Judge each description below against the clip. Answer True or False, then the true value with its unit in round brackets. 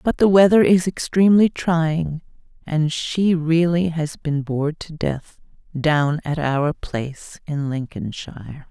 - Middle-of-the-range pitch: True (160 Hz)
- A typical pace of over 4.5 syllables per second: False (3.9 syllables/s)